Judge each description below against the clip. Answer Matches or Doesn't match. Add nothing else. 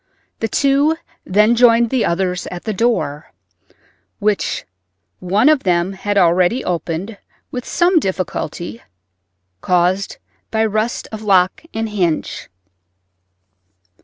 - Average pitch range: Matches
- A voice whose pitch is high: Matches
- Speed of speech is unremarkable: Doesn't match